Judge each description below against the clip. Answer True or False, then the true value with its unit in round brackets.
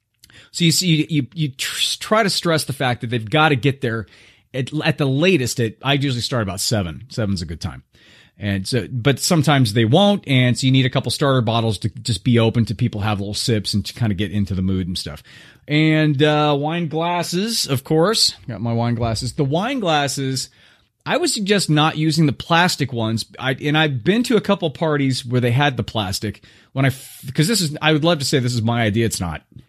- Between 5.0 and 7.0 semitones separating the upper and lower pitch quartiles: True (5.4 semitones)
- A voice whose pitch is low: True (130 Hz)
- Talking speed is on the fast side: True (230 wpm)